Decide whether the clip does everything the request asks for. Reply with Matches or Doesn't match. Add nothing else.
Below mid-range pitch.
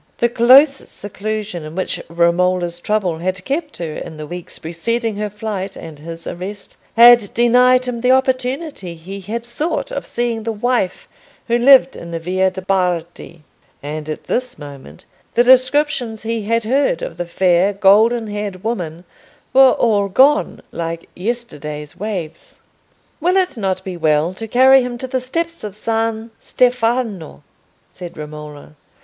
Doesn't match